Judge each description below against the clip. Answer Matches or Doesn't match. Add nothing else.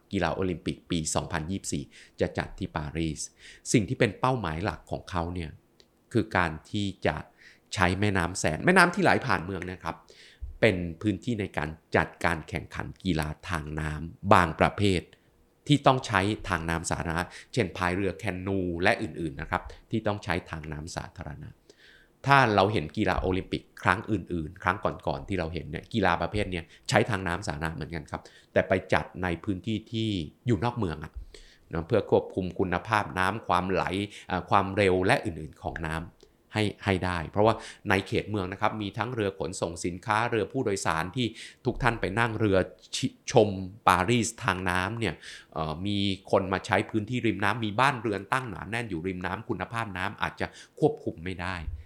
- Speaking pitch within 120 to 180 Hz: Doesn't match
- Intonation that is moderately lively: Matches